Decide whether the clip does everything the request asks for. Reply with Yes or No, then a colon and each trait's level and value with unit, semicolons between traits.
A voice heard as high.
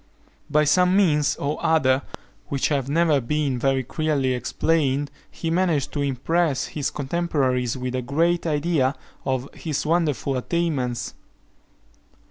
No: medium, 145 Hz